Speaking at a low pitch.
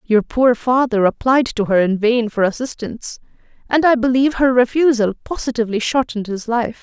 No: high, 240 Hz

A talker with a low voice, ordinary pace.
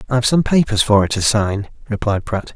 No: low, 110 Hz; fast, 210 wpm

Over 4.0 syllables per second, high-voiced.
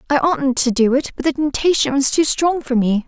Yes: 5.3 syllables/s; very high, 275 Hz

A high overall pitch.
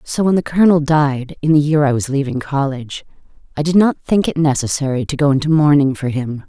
No: medium, 145 Hz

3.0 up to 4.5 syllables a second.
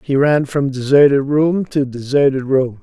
Yes: 4.4 syllables/s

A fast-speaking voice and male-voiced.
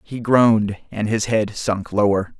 No: average, 175 wpm; male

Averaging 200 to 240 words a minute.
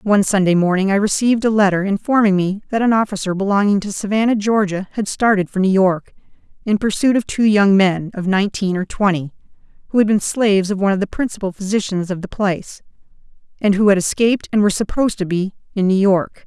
Yes: fast, 205 wpm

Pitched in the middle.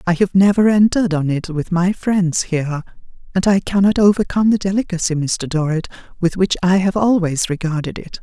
Yes: medium, 180 Hz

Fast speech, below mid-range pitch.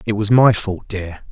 Yes: fast, 230 wpm; low, 105 Hz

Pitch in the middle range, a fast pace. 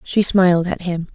Yes: medium, 180 Hz; fast, 210 wpm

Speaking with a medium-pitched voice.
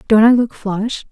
No: high, 220 Hz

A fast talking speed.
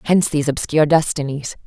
No: average, 145 wpm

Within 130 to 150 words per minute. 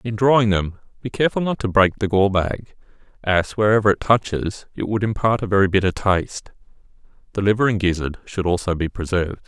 No: average, 190 wpm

